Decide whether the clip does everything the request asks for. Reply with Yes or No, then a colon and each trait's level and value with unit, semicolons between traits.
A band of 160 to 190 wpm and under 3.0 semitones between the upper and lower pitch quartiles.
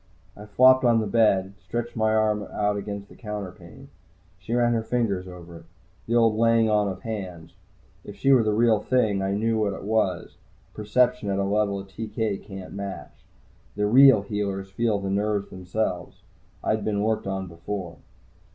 Yes: average, 180 wpm; narrow, 2.4 semitones